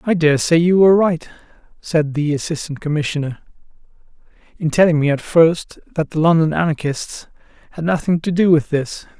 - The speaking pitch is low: No, medium, 160 Hz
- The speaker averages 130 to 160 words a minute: Yes, average, 155 wpm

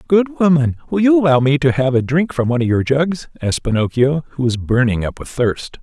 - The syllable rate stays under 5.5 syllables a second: No, 5.7 syllables/s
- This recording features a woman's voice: No, male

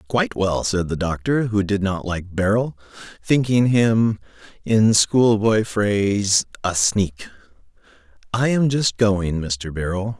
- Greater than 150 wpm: No, slow, 135 wpm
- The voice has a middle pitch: No, low, 105 Hz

